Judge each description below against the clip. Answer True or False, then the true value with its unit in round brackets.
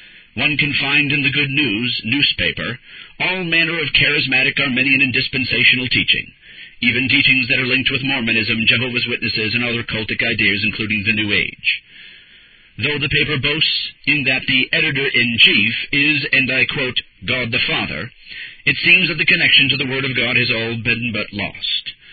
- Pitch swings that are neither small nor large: True (3.4 semitones)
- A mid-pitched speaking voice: False (130 Hz)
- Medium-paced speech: True (175 wpm)